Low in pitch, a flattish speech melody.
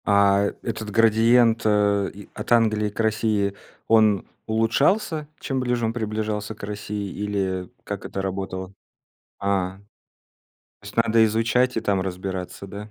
Yes: low, 105 Hz; narrow, 2.2 semitones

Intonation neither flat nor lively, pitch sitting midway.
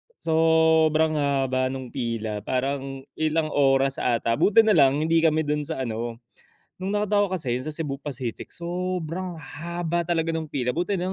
Yes: average, 4.2 semitones; medium, 155 Hz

